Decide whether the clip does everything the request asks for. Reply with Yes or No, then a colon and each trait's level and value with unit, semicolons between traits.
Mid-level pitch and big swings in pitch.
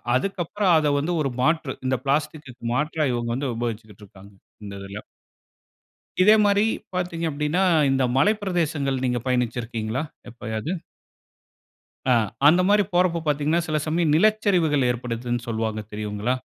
Yes: medium, 145 Hz; wide, 6.1 semitones